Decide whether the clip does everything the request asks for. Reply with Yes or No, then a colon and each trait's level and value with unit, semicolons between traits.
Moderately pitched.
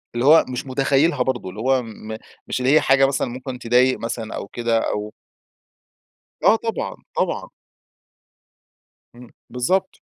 No: low, 125 Hz